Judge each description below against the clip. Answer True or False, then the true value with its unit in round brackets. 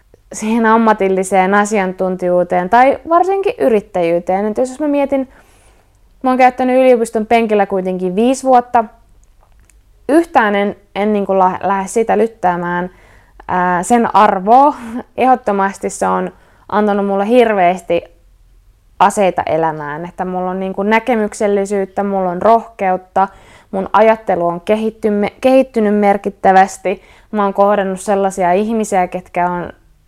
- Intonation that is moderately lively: True (3.7 semitones)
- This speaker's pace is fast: False (120 wpm)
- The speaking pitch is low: False (200 Hz)